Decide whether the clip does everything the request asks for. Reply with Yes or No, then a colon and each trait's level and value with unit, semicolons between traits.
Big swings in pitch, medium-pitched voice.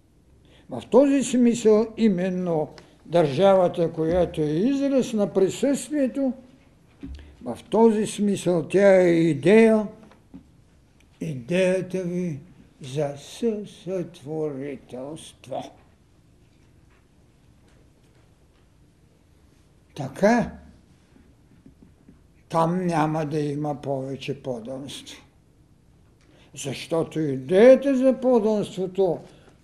Yes: wide, 5.9 semitones; medium, 175 Hz